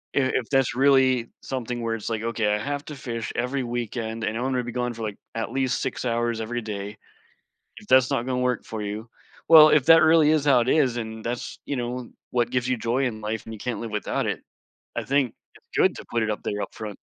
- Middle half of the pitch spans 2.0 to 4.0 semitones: Yes, average, 2.7 semitones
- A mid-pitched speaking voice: No, low, 120 Hz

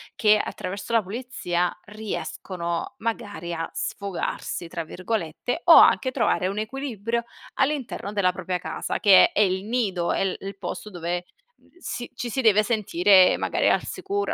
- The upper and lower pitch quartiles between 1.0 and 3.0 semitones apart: No, average, 4.2 semitones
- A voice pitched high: Yes, high, 205 Hz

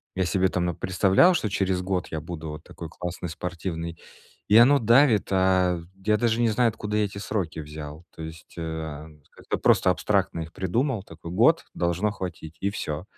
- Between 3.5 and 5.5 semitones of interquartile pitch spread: Yes, average, 4.4 semitones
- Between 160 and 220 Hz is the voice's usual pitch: No, very low, 90 Hz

